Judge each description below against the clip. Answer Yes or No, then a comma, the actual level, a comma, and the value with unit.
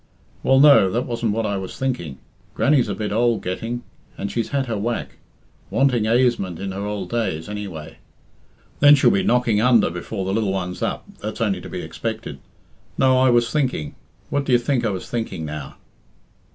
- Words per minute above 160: Yes, average, 185 wpm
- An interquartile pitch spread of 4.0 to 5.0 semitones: Yes, average, 4.4 semitones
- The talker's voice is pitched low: Yes, low, 115 Hz